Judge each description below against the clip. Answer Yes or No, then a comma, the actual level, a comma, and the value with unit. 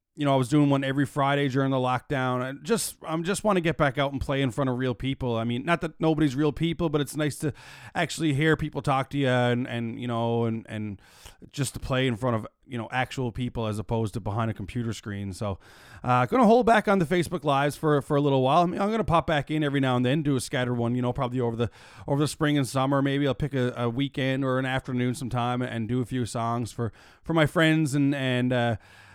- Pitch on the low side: Yes, low, 130 Hz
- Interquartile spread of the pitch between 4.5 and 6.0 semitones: No, average, 3.5 semitones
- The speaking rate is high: Yes, fast, 270 wpm